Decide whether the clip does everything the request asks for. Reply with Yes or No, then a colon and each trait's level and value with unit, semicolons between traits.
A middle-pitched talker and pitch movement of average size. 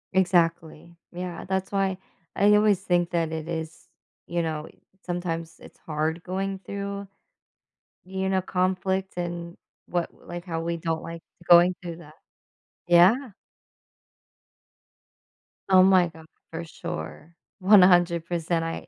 No: medium, 175 Hz; narrow, 2.3 semitones